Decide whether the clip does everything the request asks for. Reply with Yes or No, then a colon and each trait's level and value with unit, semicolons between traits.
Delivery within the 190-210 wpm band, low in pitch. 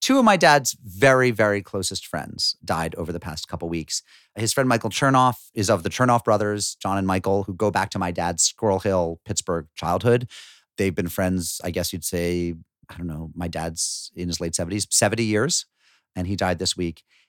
Yes: fast, 205 wpm; very low, 95 Hz